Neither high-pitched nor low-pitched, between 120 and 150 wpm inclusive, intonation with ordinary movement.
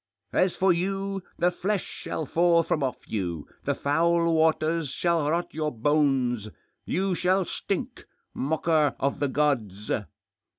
Yes: medium, 160 Hz; slow, 135 wpm; average, 4.0 semitones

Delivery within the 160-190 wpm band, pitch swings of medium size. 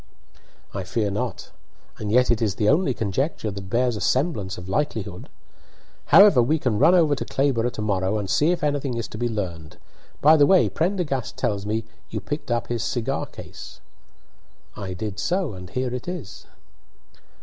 No: average, 180 wpm; wide, 5.9 semitones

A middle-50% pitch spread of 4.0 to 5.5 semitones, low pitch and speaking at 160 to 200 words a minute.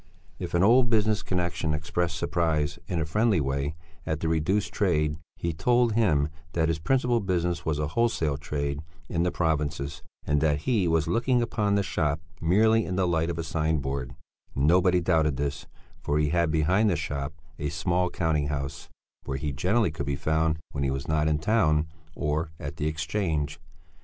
No: average, 3.4 semitones; very low, 80 Hz; average, 185 wpm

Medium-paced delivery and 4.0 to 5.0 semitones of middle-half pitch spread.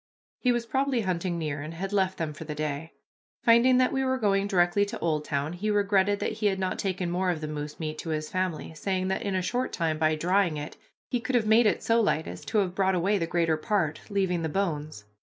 No: fast, 245 wpm; average, 4.5 semitones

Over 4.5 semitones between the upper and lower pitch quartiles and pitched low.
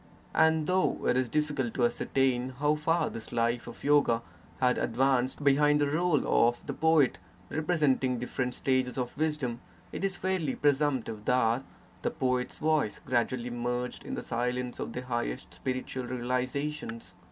No: average, 3.3 semitones; low, 130 Hz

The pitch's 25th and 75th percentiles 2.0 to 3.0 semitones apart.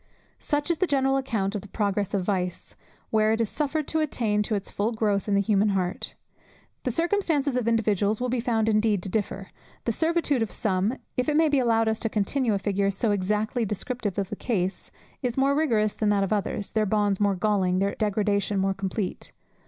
No: average, 3.8 semitones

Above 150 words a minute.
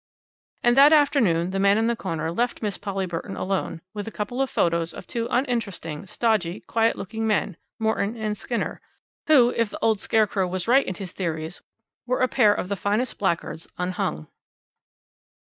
Yes: average, 180 wpm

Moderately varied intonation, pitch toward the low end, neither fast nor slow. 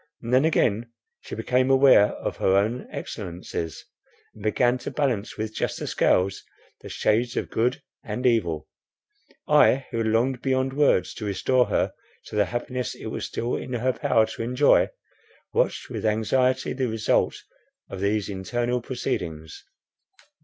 Yes: average, 3.3 semitones; low, 115 Hz; average, 150 wpm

